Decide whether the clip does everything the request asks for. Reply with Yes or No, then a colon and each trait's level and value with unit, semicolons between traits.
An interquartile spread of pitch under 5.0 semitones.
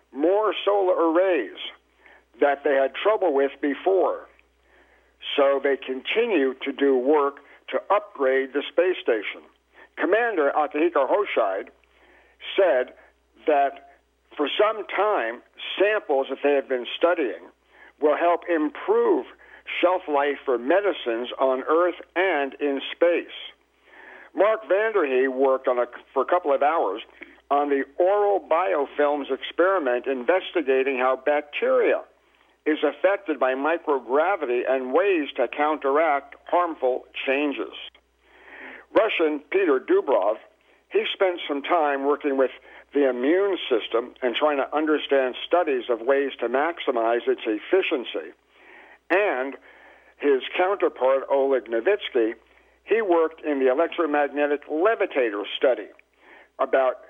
No: wide, 5.6 semitones